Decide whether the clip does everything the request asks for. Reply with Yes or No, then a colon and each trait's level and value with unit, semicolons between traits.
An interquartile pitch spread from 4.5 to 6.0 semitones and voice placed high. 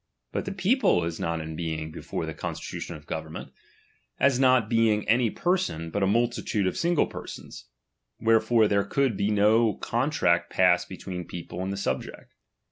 No: wide, 5.5 semitones; low, 105 Hz